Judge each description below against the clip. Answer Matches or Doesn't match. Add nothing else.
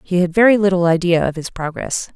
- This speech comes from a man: Doesn't match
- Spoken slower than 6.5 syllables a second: Matches